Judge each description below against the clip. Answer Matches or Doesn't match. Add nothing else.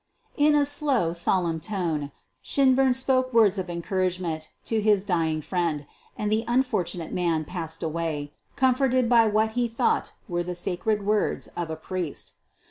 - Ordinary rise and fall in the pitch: Doesn't match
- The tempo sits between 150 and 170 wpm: Matches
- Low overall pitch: Doesn't match